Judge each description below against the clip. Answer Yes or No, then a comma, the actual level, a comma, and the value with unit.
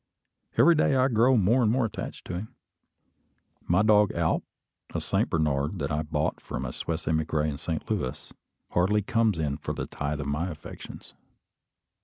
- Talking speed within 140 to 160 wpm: No, average, 175 wpm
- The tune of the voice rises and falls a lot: Yes, wide, 6.4 semitones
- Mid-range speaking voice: No, very low, 85 Hz